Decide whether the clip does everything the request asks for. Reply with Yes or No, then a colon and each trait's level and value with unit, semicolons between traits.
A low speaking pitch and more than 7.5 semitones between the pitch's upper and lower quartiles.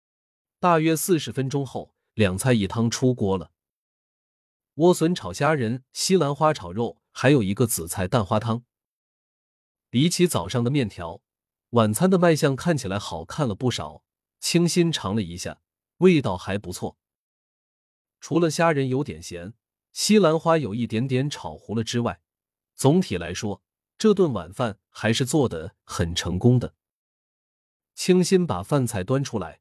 Yes: low, 120 Hz; wide, 8.0 semitones